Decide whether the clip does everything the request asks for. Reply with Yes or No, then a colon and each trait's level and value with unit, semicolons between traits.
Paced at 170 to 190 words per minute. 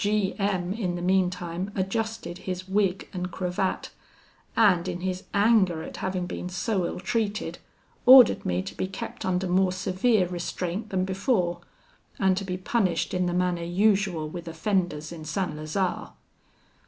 No: average, 155 wpm